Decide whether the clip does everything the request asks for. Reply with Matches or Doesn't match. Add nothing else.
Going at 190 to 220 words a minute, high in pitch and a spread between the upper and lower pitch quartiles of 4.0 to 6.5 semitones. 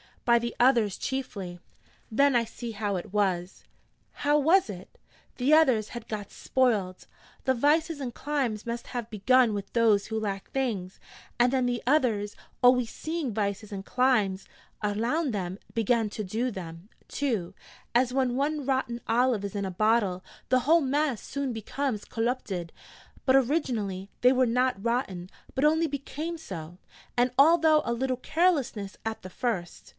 Doesn't match